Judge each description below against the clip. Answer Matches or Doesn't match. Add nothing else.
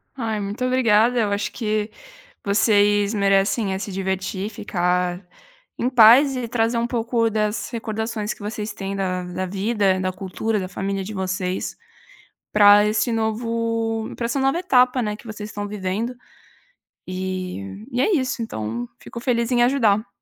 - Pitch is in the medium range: Doesn't match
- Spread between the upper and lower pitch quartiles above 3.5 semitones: Doesn't match